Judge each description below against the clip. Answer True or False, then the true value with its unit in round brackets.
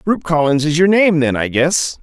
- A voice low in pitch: False (160 Hz)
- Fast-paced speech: True (240 wpm)